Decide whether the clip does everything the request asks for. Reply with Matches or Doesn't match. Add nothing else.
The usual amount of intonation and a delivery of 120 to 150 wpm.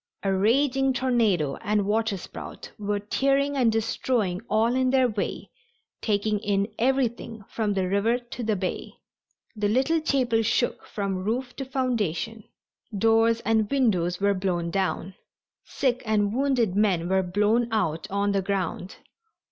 Matches